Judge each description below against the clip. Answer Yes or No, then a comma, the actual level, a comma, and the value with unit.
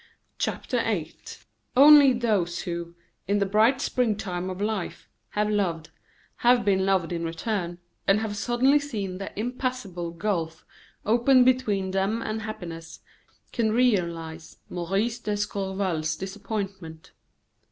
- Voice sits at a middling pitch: No, high, 200 Hz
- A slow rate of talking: Yes, slow, 120 wpm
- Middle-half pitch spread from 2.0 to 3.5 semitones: No, average, 4.4 semitones